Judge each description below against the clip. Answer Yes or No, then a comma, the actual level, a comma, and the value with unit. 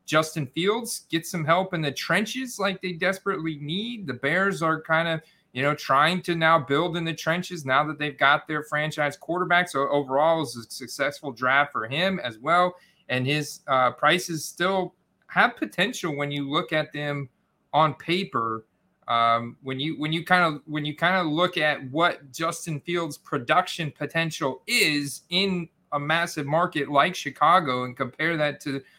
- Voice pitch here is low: No, medium, 160 Hz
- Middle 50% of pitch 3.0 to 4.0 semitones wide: Yes, average, 3.5 semitones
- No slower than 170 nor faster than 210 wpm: Yes, average, 180 wpm